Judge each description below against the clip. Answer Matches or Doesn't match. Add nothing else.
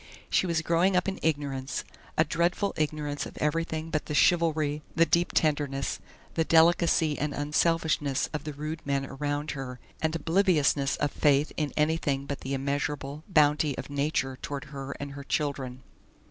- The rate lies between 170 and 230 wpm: Doesn't match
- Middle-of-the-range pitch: Matches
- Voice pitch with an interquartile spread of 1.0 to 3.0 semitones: Matches